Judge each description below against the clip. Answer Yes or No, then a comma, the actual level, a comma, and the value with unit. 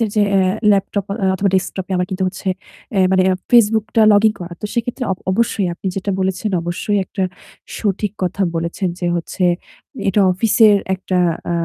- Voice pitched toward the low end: No, high, 195 Hz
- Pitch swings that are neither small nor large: No, narrow, 2.2 semitones